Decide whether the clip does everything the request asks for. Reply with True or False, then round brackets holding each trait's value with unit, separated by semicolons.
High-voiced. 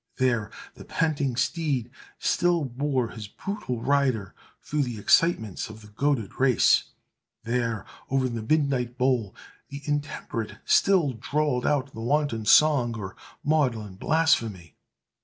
False (130 Hz)